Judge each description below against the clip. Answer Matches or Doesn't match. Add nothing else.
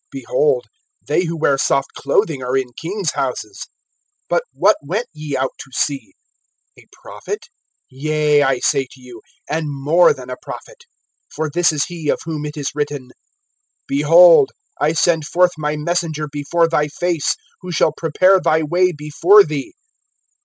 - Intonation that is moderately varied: Matches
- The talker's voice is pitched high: Doesn't match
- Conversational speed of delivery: Matches